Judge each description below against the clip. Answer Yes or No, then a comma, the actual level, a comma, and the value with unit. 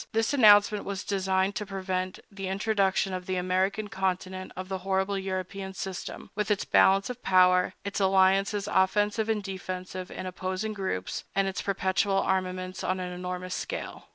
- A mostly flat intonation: Yes, narrow, 1.3 semitones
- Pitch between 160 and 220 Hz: Yes, high, 190 Hz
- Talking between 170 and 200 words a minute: No, average, 155 wpm